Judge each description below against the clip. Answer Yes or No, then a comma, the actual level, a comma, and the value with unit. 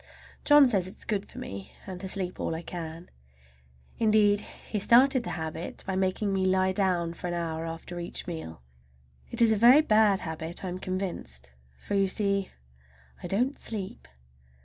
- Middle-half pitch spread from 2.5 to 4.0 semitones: Yes, average, 3.5 semitones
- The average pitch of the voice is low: No, high, 190 Hz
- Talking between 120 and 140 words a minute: No, average, 180 wpm